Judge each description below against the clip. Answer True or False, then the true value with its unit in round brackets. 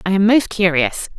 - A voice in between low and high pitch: False (195 Hz)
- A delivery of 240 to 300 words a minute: False (205 wpm)